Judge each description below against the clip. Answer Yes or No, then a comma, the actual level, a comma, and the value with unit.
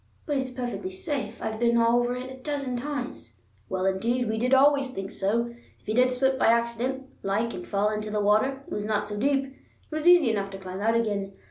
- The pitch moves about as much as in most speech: Yes, average, 4.0 semitones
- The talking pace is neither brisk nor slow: No, fast, 230 wpm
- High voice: Yes, high, 235 Hz